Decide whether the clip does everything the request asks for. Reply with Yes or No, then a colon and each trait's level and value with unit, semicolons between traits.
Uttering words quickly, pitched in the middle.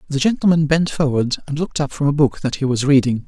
Yes: fast, 255 wpm; medium, 145 Hz